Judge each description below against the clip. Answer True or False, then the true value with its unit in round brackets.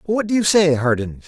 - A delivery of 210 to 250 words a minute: True (235 wpm)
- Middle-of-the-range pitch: True (160 Hz)